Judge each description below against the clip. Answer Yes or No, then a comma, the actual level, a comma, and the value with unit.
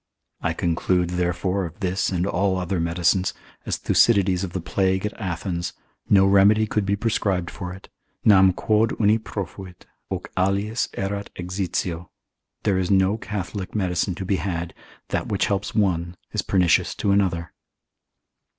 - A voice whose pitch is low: Yes, very low, 95 Hz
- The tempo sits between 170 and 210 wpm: No, average, 150 wpm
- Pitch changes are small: Yes, narrow, 2.1 semitones